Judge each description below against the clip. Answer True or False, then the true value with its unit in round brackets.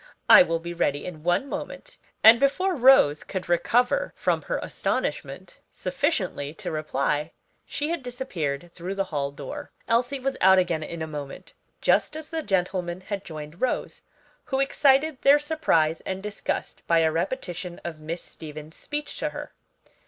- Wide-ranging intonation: True (9.0 semitones)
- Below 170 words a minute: True (160 wpm)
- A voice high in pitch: False (180 Hz)